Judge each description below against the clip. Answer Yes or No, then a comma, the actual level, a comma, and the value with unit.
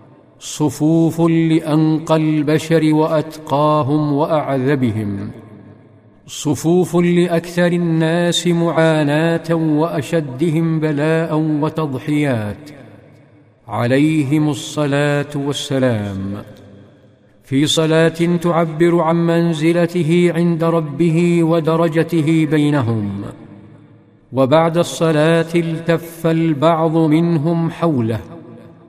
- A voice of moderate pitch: Yes, medium, 155 Hz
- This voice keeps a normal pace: No, slow, 60 wpm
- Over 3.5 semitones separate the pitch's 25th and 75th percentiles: No, average, 2.9 semitones